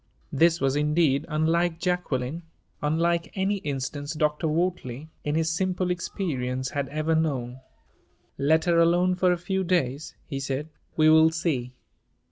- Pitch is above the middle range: No, medium, 160 Hz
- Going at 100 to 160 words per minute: Yes, average, 140 wpm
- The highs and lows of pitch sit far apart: No, average, 3.4 semitones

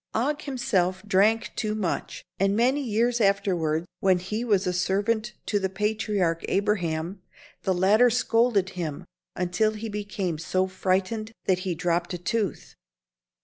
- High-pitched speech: Yes, high, 200 Hz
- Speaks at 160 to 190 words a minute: No, average, 145 wpm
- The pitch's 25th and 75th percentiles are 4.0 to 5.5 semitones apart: No, average, 3.3 semitones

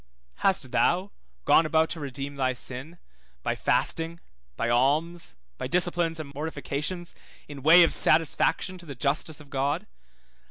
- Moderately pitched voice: Yes, medium, 155 Hz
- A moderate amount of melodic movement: Yes, average, 3.4 semitones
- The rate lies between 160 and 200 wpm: No, average, 145 wpm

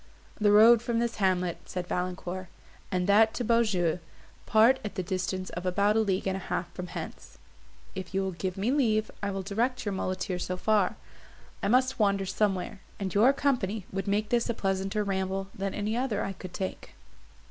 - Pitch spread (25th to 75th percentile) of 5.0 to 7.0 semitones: No, average, 2.7 semitones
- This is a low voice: No, high, 195 Hz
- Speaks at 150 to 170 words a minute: No, average, 190 wpm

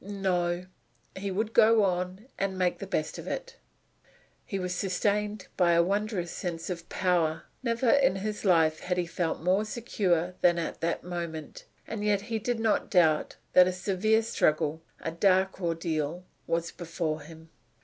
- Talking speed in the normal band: Yes, average, 165 wpm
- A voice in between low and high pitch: Yes, medium, 180 Hz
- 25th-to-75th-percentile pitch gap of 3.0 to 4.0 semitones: Yes, average, 3.4 semitones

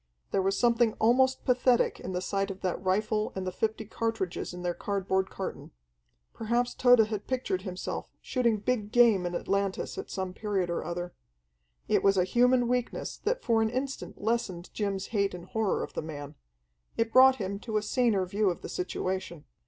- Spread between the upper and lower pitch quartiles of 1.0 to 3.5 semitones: No, average, 4.0 semitones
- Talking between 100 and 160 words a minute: No, average, 185 wpm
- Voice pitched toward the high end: Yes, high, 205 Hz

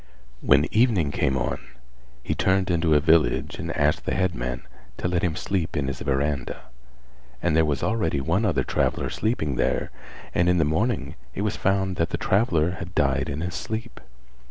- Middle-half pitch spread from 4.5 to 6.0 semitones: Yes, average, 4.9 semitones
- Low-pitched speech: Yes, very low, 80 Hz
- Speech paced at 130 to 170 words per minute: No, average, 180 wpm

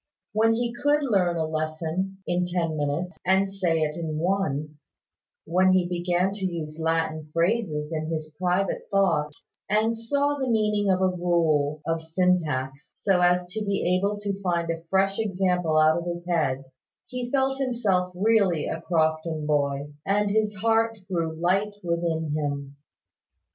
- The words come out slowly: No, average, 160 wpm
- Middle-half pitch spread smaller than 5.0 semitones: Yes, average, 3.9 semitones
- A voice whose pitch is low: No, medium, 175 Hz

